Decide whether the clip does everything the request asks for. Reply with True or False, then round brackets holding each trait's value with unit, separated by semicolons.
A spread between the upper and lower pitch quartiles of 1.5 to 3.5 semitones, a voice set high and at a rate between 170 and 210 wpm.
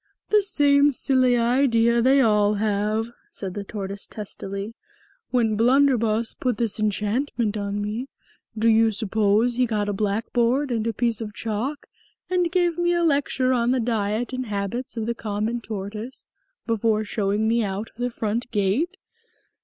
False (3.2 semitones; 225 Hz; 160 wpm)